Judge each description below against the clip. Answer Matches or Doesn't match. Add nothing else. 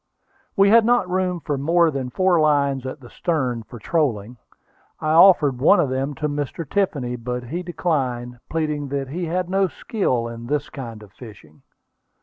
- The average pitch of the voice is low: Doesn't match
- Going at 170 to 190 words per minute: Matches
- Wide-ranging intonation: Matches